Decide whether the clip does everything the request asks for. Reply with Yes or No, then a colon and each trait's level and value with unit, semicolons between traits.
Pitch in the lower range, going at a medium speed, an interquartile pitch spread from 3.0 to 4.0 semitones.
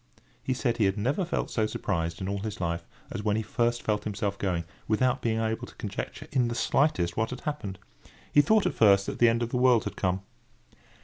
No: low, 110 Hz; fast, 230 wpm; average, 3.6 semitones